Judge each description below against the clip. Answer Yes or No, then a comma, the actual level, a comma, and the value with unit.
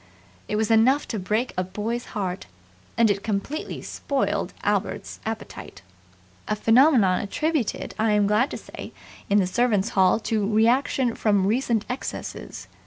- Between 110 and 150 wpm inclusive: Yes, average, 145 wpm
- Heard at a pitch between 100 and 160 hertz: No, high, 220 Hz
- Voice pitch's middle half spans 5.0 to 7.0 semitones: No, average, 3.1 semitones